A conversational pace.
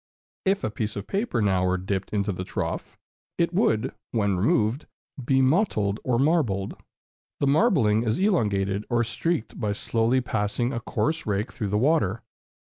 Yes: average, 160 wpm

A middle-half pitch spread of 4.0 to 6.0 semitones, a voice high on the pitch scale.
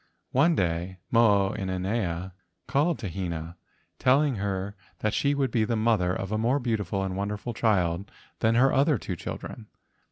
No: average, 4.4 semitones; low, 105 Hz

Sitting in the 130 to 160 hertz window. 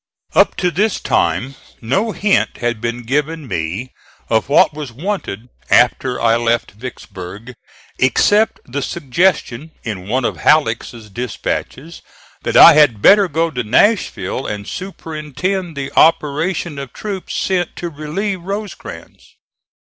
Yes: medium, 140 Hz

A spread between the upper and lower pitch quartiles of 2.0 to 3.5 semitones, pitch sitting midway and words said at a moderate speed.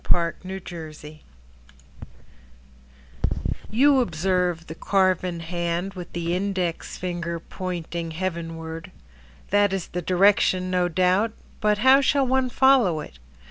No: average, 2.7 semitones; medium, 180 Hz; slow, 110 wpm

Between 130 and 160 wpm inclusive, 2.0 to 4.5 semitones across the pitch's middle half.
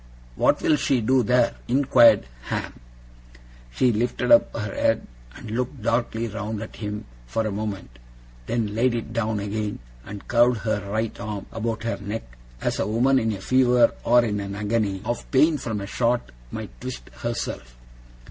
No: average, 170 wpm; average, 2.7 semitones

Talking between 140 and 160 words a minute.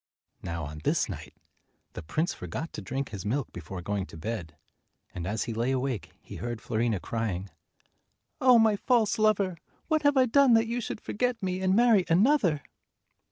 No: average, 180 wpm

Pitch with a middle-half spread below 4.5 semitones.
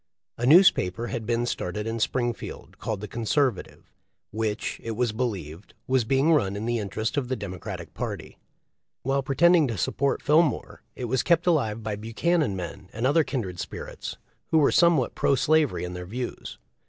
No: average, 4.8 semitones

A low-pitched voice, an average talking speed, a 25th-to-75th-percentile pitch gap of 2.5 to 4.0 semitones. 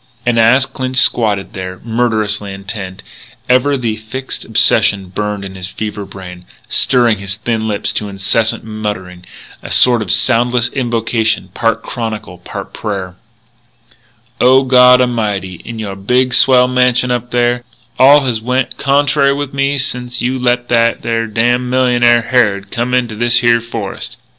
Yes: low, 115 Hz; average, 150 wpm; average, 3.3 semitones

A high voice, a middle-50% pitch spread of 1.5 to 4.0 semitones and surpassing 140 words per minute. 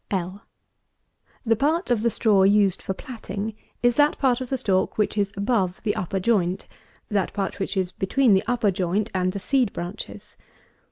Yes: high, 205 Hz; average, 3.7 semitones; average, 175 wpm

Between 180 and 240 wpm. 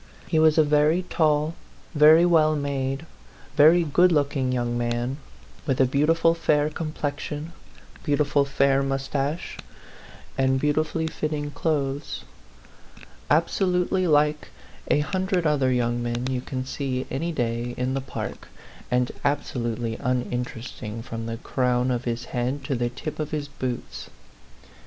No: slow, 135 wpm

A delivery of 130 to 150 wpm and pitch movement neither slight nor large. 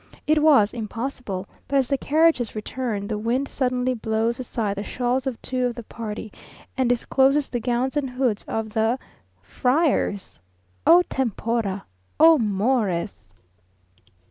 Yes: average, 140 wpm; average, 3.5 semitones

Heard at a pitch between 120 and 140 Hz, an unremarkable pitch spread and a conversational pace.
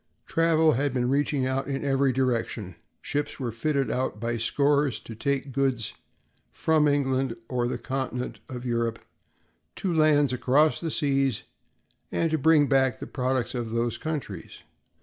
Yes: low, 135 Hz; average, 3.0 semitones; average, 150 wpm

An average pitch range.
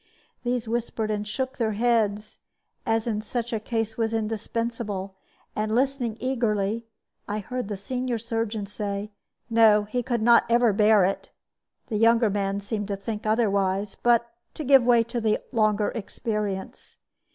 No: narrow, 2.2 semitones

